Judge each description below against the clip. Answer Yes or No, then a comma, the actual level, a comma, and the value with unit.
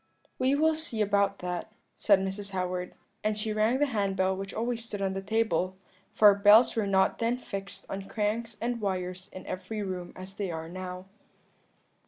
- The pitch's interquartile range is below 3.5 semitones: Yes, average, 2.8 semitones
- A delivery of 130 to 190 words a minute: Yes, average, 185 wpm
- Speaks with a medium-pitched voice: No, high, 200 Hz